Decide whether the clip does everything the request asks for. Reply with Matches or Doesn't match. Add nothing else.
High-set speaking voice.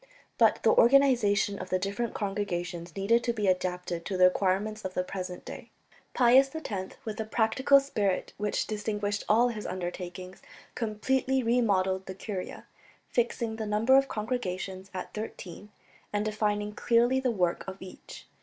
Matches